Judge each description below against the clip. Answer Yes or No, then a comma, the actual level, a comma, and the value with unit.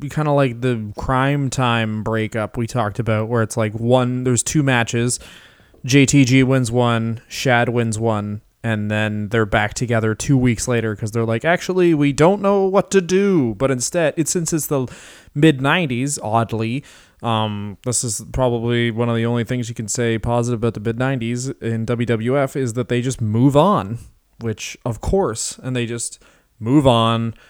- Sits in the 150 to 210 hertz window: No, low, 120 Hz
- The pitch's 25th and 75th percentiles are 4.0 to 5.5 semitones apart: No, average, 3.0 semitones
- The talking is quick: No, average, 180 wpm